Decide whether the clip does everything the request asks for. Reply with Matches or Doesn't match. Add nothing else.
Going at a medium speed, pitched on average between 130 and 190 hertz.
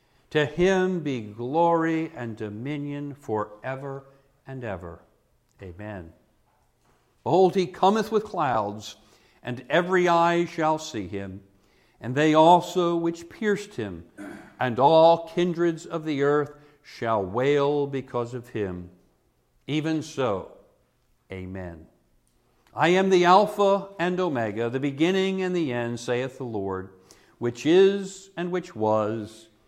Doesn't match